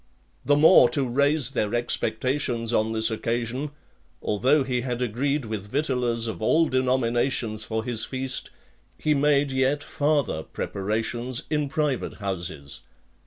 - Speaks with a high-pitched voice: No, low, 125 Hz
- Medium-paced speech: No, slow, 130 wpm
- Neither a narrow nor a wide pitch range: Yes, average, 4.0 semitones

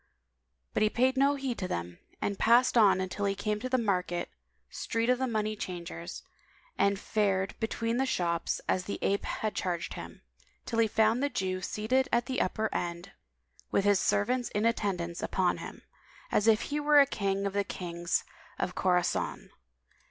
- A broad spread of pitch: No, average, 4.2 semitones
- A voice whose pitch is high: Yes, high, 205 Hz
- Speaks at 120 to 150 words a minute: No, average, 175 wpm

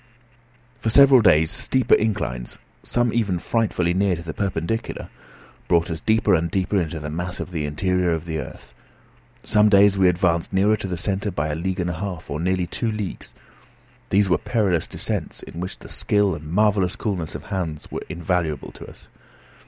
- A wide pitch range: No, average, 3.6 semitones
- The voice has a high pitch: No, very low, 90 Hz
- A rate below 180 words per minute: No, average, 185 wpm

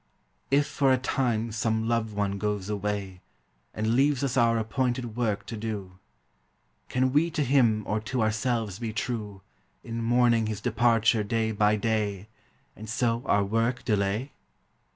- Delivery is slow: No, average, 150 wpm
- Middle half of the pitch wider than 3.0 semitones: No, narrow, 2.6 semitones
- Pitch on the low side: Yes, low, 110 Hz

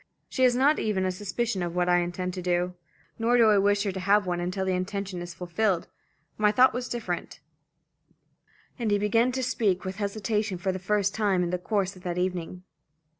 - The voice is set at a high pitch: Yes, high, 195 Hz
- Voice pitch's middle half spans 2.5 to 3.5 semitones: Yes, average, 2.9 semitones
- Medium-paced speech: No, fast, 210 wpm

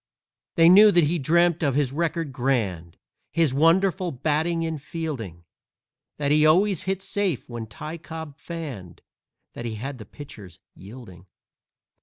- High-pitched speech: No, medium, 150 Hz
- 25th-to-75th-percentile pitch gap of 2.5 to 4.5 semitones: No, wide, 5.4 semitones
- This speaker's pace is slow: No, average, 145 wpm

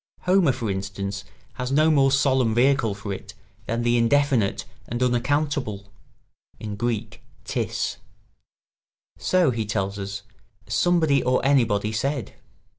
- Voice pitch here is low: Yes, low, 120 Hz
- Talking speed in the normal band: No, slow, 115 wpm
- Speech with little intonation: No, average, 5.1 semitones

